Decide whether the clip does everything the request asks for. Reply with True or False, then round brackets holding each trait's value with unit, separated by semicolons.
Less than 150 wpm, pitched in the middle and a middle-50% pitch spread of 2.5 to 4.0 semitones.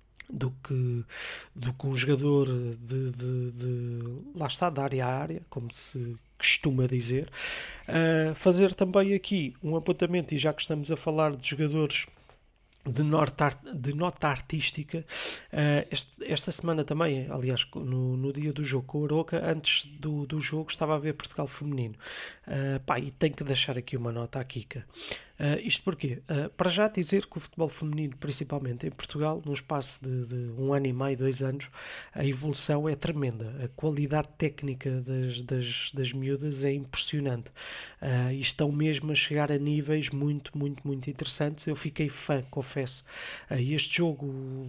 False (175 wpm; 145 Hz; 2.8 semitones)